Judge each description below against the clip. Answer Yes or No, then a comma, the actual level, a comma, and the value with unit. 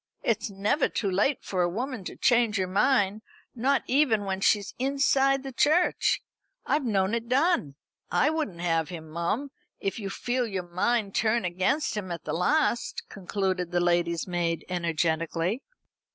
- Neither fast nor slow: Yes, average, 160 wpm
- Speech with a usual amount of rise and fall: No, wide, 6.4 semitones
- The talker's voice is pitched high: Yes, high, 200 Hz